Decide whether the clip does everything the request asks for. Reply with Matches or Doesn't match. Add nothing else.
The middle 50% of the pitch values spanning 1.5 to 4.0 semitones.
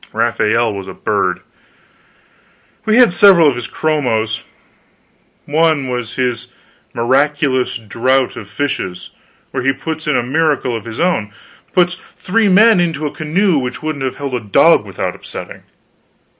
Doesn't match